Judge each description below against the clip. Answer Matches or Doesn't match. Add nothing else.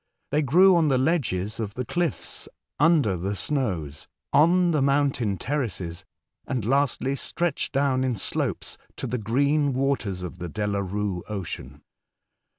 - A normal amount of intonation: Doesn't match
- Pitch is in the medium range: Doesn't match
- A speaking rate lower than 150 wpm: Matches